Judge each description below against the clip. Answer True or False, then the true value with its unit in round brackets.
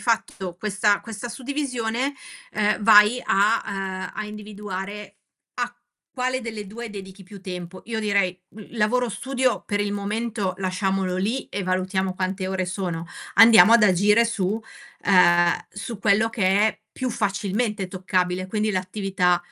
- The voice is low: False (205 Hz)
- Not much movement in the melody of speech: False (3.0 semitones)